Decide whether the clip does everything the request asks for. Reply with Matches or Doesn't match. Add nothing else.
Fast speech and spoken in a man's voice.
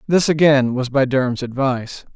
Doesn't match